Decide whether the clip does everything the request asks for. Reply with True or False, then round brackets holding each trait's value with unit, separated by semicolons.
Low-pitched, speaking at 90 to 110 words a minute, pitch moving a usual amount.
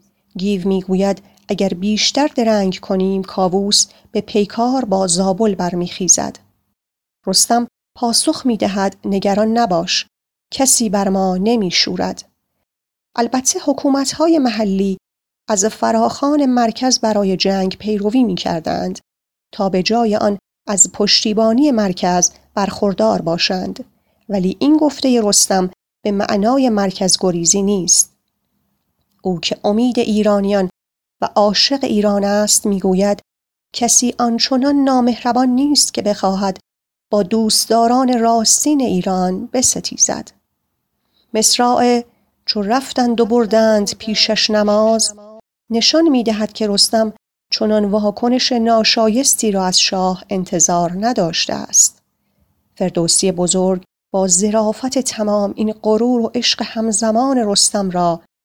False (215 Hz; 105 wpm; 3.5 semitones)